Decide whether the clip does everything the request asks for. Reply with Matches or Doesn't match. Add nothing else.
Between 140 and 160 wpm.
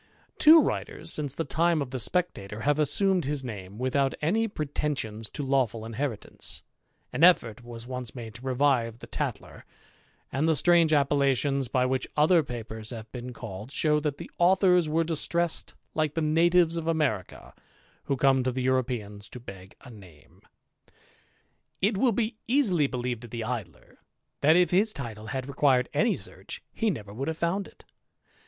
Doesn't match